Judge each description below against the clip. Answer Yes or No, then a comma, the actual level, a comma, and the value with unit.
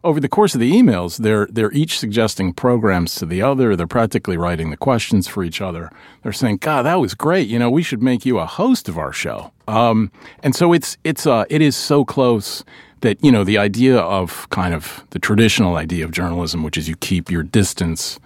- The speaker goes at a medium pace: No, fast, 225 wpm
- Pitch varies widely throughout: Yes, wide, 7.1 semitones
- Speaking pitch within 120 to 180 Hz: No, low, 110 Hz